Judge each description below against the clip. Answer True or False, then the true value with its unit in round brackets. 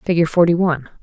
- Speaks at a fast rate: False (175 wpm)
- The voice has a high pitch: False (165 Hz)